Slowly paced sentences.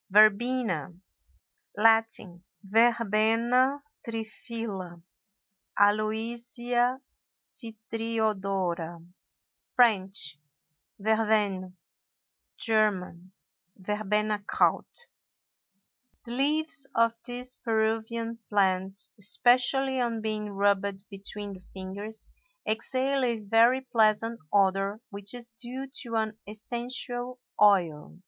Yes: slow, 70 wpm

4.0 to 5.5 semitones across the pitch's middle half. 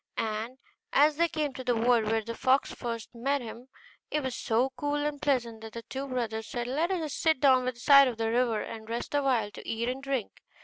No: average, 3.3 semitones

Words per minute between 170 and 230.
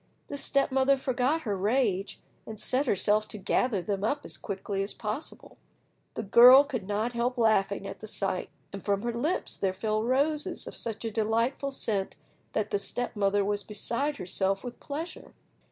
Yes: average, 180 wpm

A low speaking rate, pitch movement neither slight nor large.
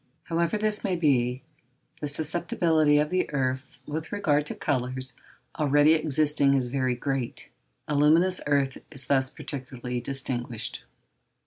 Yes: slow, 125 wpm; average, 3.2 semitones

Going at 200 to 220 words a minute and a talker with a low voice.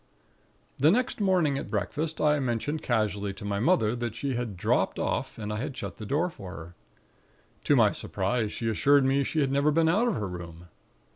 Yes: fast, 205 wpm; low, 125 Hz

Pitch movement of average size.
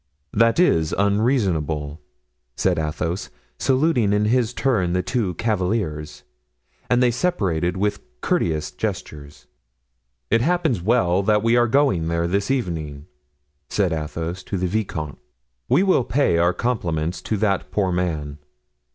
No: wide, 5.9 semitones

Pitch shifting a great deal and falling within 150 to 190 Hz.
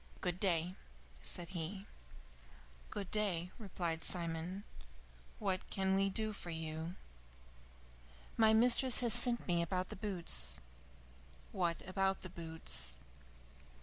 No: average, 3.2 semitones; medium, 185 Hz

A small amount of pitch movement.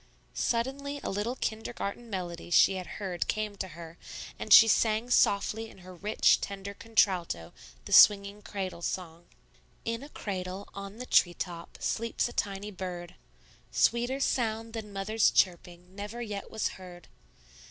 No: average, 3.6 semitones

